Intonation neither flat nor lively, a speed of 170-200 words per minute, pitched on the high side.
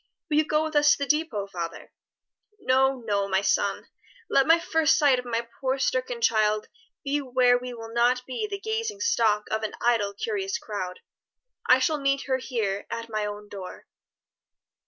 No: wide, 5.9 semitones; average, 180 wpm; very high, 255 Hz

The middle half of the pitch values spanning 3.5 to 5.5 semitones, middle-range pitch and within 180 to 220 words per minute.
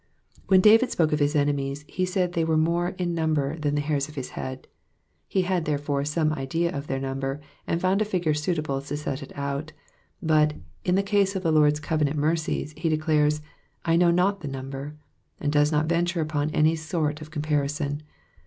No: average, 2.7 semitones; medium, 155 Hz; average, 200 wpm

